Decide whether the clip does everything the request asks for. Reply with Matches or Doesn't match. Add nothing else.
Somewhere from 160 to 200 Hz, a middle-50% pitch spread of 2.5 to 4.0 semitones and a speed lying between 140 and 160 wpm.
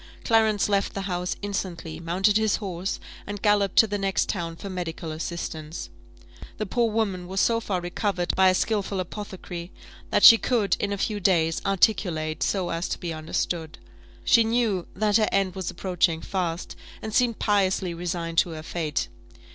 Doesn't match